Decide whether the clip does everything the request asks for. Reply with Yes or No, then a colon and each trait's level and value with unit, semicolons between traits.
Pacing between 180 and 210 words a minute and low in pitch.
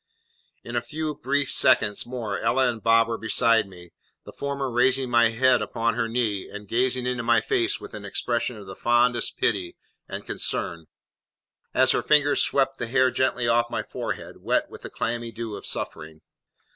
Yes: average, 185 wpm; low, 120 Hz